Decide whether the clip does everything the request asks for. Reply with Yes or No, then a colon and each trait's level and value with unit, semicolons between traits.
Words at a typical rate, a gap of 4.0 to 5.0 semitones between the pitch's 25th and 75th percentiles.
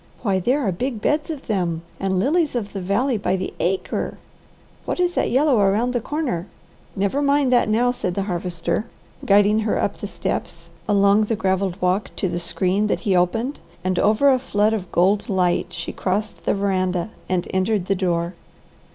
Yes: average, 185 wpm; average, 4.5 semitones